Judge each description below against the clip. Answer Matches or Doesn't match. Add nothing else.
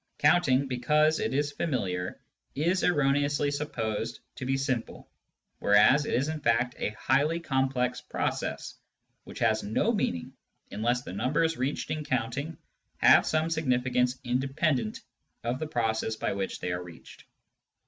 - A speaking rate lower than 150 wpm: Matches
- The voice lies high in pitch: Doesn't match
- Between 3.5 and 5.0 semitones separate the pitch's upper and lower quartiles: Matches